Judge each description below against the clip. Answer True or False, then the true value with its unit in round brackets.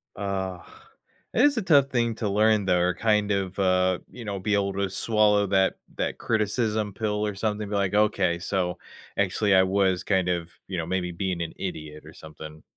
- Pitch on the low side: True (100 Hz)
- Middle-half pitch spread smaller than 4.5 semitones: True (2.4 semitones)